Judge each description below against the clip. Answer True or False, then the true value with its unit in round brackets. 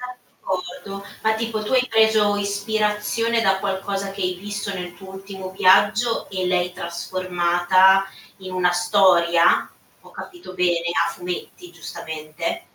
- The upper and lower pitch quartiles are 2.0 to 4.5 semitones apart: True (2.7 semitones)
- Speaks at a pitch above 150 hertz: True (190 Hz)